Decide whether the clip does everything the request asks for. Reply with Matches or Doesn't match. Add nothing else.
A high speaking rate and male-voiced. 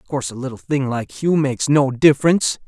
Matches